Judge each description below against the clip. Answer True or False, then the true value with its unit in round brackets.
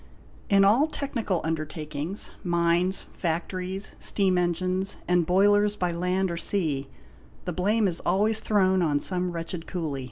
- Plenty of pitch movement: False (2.6 semitones)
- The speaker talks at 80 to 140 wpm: True (135 wpm)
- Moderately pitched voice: True (180 Hz)